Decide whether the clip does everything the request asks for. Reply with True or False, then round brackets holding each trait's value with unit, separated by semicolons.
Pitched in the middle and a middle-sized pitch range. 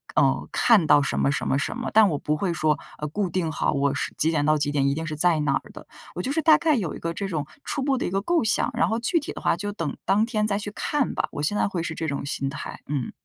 False (170 Hz; 6.2 semitones)